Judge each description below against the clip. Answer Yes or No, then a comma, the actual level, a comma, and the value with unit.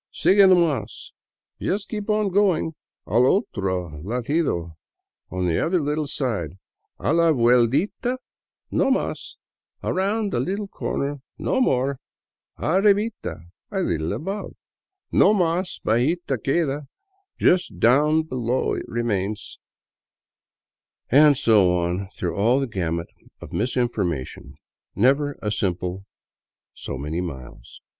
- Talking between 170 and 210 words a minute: No, slow, 135 wpm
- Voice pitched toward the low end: Yes, low, 130 Hz